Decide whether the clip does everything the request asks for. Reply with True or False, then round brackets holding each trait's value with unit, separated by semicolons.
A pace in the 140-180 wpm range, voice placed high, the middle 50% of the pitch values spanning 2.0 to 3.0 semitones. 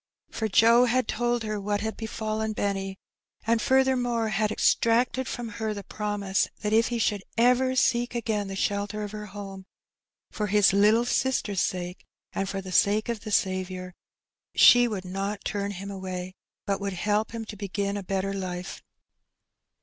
True (170 wpm; 210 Hz; 2.6 semitones)